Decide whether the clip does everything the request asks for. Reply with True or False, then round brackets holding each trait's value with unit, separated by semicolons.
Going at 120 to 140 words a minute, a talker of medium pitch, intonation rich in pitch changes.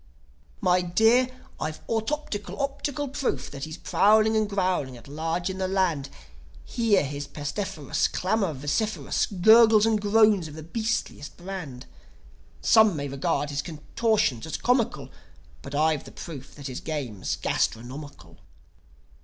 True (135 wpm; 180 Hz; 7.1 semitones)